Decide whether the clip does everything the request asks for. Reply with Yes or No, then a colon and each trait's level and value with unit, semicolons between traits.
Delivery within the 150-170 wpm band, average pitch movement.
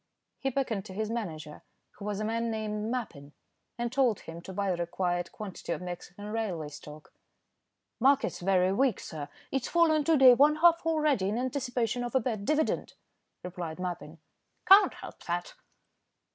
No: average, 165 wpm; wide, 6.4 semitones